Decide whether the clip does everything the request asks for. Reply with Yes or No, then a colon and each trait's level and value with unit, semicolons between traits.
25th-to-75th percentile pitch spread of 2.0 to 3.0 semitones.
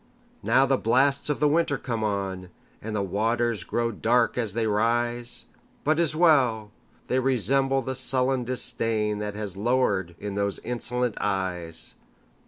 No: average, 3.9 semitones